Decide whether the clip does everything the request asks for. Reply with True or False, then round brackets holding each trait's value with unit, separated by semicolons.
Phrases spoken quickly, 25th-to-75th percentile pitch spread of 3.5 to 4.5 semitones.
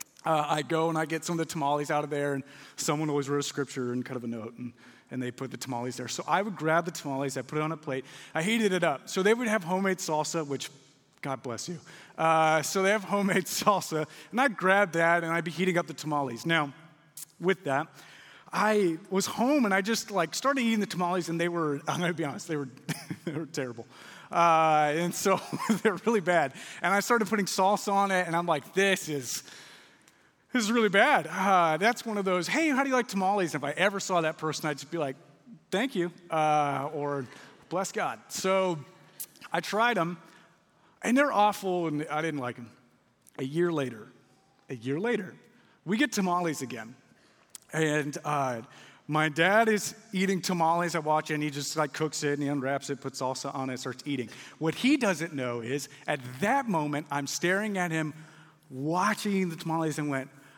False (210 wpm; 4.9 semitones)